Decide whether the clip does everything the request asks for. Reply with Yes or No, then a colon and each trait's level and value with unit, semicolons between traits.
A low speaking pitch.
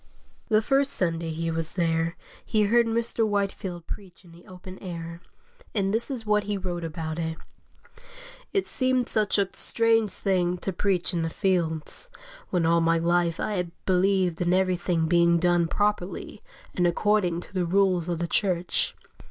No: medium, 180 Hz